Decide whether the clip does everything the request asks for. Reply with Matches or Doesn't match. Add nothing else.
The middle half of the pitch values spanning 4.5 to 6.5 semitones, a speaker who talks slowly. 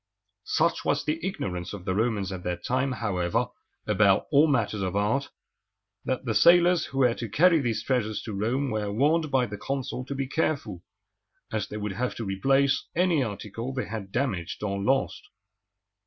Doesn't match